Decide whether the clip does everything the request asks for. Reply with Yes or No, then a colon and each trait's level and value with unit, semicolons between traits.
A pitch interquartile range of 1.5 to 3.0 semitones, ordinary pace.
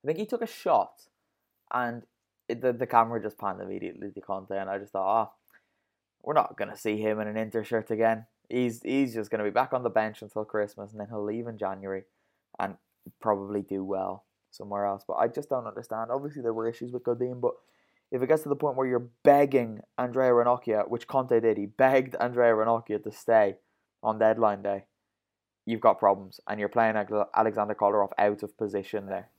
No: average, 2.7 semitones; fast, 210 wpm